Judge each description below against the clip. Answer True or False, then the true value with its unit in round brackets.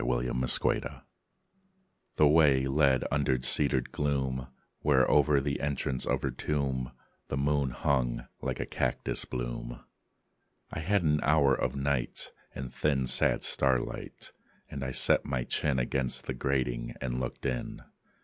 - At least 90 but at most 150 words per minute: True (145 wpm)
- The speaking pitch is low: True (65 Hz)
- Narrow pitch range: True (2.1 semitones)